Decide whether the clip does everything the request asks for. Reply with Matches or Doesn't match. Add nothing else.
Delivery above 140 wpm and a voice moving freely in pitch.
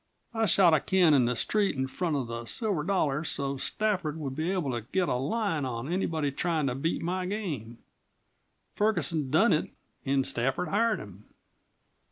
Matches